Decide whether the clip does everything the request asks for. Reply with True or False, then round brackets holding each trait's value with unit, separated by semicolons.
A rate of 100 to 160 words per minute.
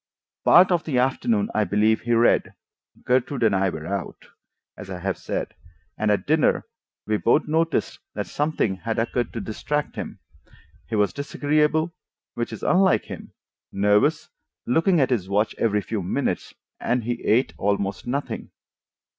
True (155 wpm)